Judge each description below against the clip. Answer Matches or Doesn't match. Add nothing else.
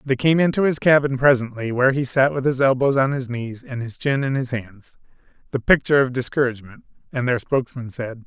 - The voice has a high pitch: Doesn't match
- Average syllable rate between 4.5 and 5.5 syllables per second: Doesn't match